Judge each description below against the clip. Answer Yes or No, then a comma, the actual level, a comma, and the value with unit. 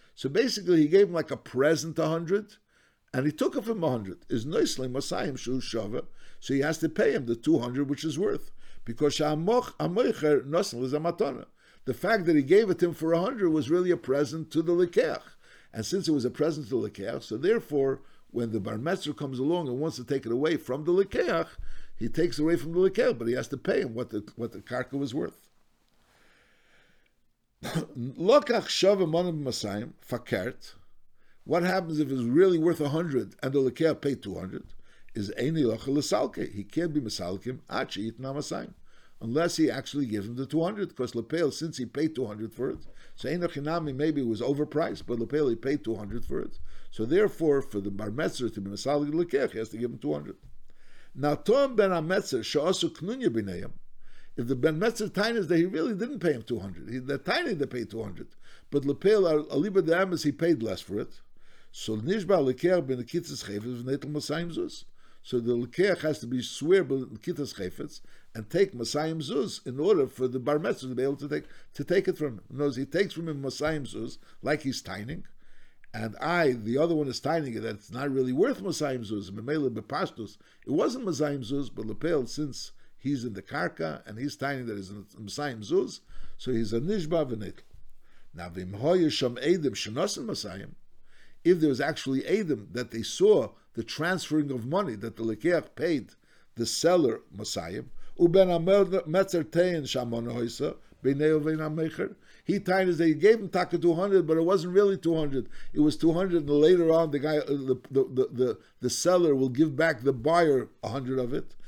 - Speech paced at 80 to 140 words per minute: No, average, 185 wpm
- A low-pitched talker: No, medium, 145 Hz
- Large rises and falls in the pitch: Yes, wide, 5.7 semitones